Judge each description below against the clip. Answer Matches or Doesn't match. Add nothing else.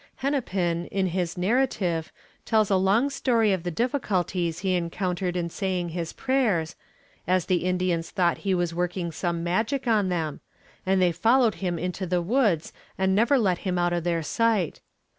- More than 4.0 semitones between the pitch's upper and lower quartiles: Doesn't match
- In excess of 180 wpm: Doesn't match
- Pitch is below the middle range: Doesn't match